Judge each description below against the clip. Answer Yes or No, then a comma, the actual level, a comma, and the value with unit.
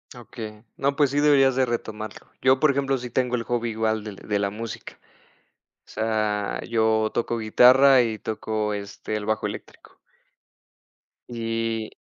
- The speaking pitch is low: Yes, low, 115 Hz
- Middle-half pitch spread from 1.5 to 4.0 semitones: Yes, average, 2.8 semitones